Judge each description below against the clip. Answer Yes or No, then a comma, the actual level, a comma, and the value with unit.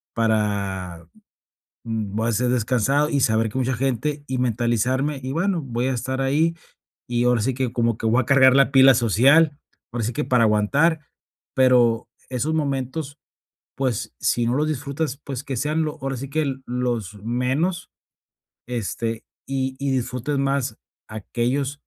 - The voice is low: Yes, low, 130 Hz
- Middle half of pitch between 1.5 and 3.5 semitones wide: Yes, average, 3.1 semitones